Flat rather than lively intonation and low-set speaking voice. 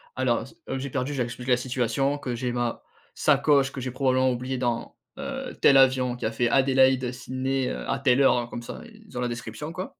Yes: narrow, 1.7 semitones; low, 130 Hz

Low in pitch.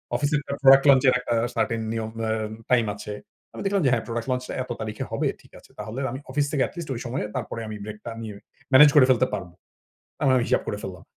Yes: low, 125 Hz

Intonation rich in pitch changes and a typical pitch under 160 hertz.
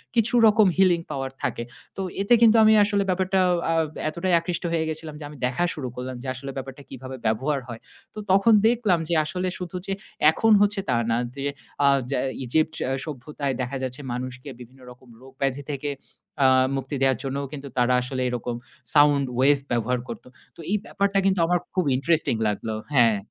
Yes: wide, 5.9 semitones; medium, 140 Hz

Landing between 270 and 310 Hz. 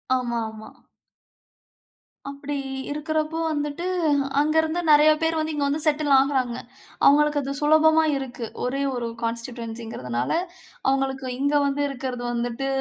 Yes: very high, 280 Hz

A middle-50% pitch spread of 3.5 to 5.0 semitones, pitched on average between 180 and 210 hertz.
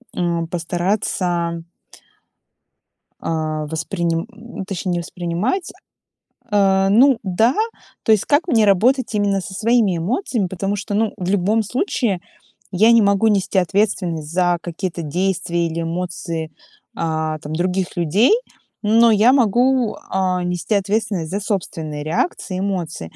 Yes: average, 3.9 semitones; high, 190 Hz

